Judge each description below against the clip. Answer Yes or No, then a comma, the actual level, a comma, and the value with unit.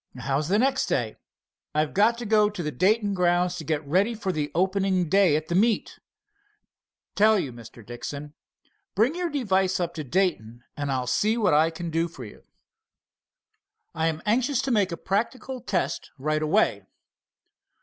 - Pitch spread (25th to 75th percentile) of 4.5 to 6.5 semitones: Yes, wide, 5.6 semitones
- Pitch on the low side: No, medium, 180 Hz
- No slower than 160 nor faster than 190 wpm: Yes, average, 170 wpm